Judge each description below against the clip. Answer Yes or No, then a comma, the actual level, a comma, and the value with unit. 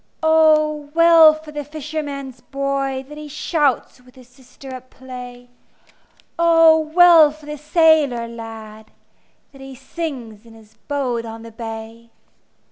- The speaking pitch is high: Yes, very high, 275 Hz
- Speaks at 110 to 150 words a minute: Yes, slow, 135 wpm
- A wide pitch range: No, average, 4.0 semitones